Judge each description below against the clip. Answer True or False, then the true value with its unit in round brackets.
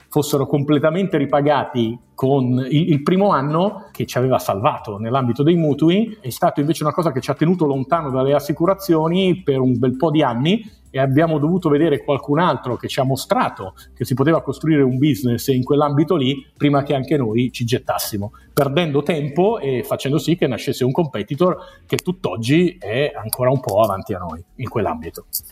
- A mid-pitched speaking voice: True (145 Hz)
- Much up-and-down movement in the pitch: False (4.2 semitones)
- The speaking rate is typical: False (180 wpm)